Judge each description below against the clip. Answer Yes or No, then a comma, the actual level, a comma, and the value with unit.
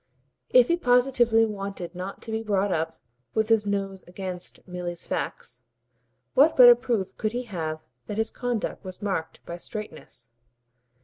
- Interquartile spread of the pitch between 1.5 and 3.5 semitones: No, average, 4.2 semitones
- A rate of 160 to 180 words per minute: No, average, 150 wpm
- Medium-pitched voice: No, high, 200 Hz